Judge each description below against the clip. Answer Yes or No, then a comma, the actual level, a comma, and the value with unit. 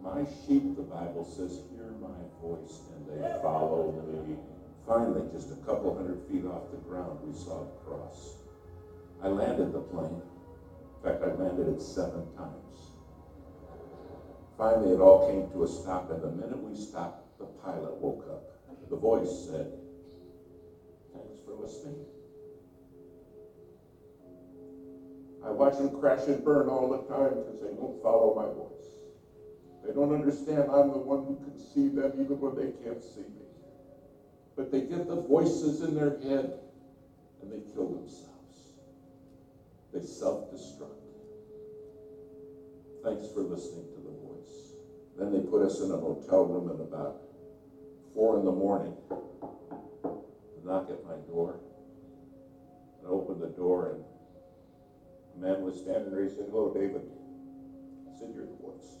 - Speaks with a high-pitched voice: No, low, 135 Hz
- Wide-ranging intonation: Yes, wide, 7.9 semitones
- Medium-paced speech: Yes, average, 145 wpm